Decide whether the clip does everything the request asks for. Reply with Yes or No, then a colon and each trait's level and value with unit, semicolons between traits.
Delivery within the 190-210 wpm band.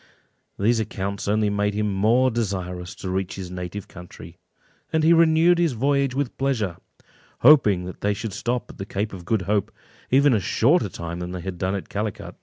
Yes: average, 195 wpm